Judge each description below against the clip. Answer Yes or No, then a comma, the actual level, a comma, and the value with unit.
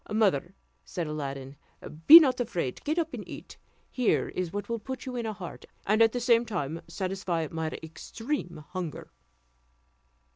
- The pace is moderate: Yes, average, 155 wpm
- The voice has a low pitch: No, high, 195 Hz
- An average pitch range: No, wide, 6.4 semitones